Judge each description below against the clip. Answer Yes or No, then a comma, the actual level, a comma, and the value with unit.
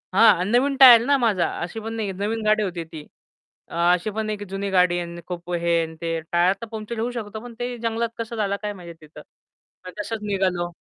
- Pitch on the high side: Yes, high, 205 Hz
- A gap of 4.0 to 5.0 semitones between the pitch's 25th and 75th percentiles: Yes, average, 4.3 semitones